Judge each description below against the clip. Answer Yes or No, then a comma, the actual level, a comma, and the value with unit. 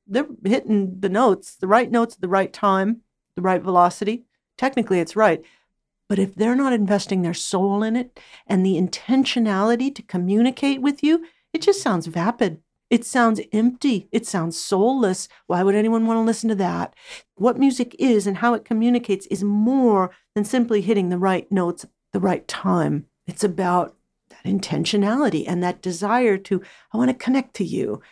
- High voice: Yes, high, 215 Hz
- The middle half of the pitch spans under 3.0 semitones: No, average, 4.3 semitones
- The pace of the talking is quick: No, average, 180 wpm